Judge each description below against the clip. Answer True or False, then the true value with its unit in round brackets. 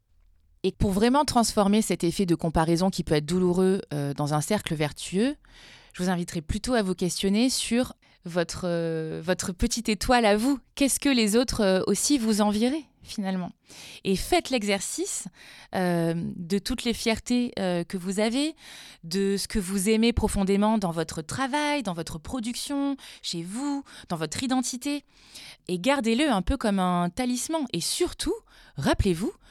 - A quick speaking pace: False (165 wpm)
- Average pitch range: False (6.2 semitones)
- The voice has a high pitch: True (205 Hz)